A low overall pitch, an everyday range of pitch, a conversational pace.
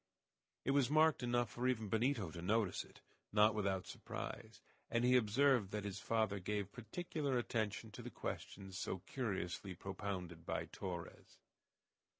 Yes: low, 105 Hz; average, 4.1 semitones; average, 150 wpm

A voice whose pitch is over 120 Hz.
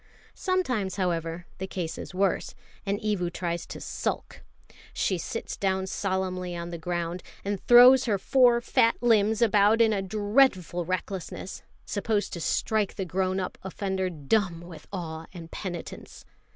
Yes: high, 190 Hz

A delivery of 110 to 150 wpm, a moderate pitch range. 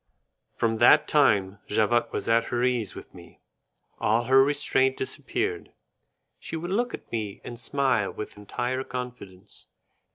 Yes: average, 140 wpm; average, 3.8 semitones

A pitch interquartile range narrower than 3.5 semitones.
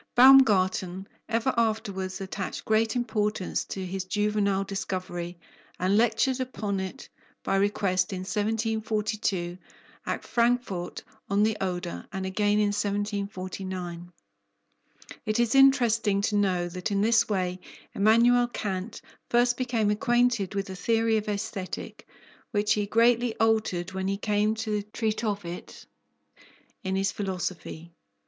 Yes: average, 2.9 semitones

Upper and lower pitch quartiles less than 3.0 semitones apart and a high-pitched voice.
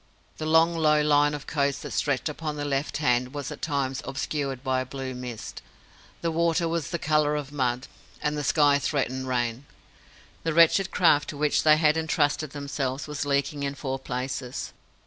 No: narrow, 2.4 semitones; medium, 145 Hz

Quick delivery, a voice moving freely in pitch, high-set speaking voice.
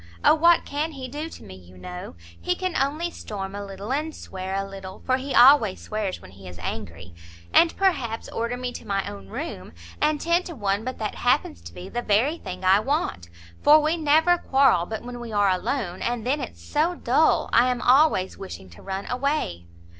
Yes: fast, 210 wpm; wide, 7.7 semitones; high, 235 Hz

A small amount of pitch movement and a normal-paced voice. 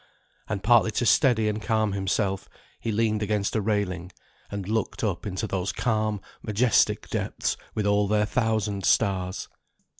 Yes: narrow, 1.9 semitones; average, 150 wpm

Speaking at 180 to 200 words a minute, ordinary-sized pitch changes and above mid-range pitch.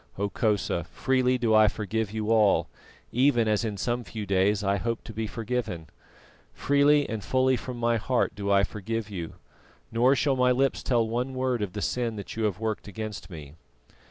No: average, 185 wpm; average, 3.3 semitones; low, 110 Hz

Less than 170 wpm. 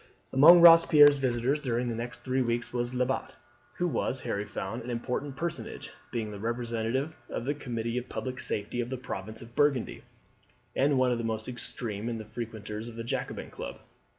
No: average, 185 wpm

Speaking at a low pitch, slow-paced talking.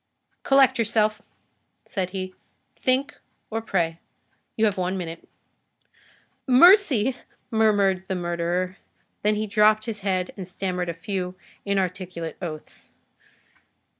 No: high, 195 Hz; slow, 110 wpm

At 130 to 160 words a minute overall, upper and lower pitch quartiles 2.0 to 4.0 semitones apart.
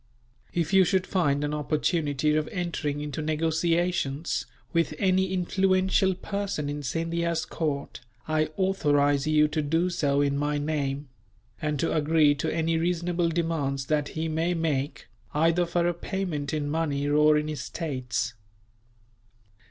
Yes: average, 140 wpm; average, 2.8 semitones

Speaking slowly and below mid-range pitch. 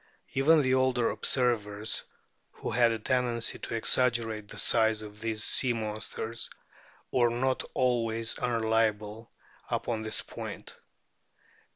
Yes: slow, 115 wpm; low, 115 Hz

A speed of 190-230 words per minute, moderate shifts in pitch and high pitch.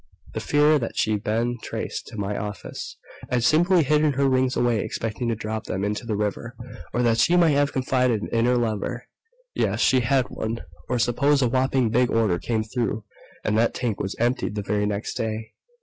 No: average, 195 wpm; average, 3.0 semitones; low, 120 Hz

